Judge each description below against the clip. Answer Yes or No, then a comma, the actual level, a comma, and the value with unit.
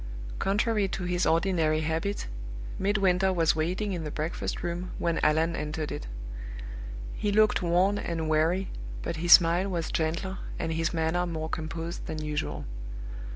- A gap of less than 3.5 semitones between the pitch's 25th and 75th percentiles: Yes, average, 2.9 semitones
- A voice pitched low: No, medium, 170 Hz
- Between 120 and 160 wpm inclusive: Yes, average, 150 wpm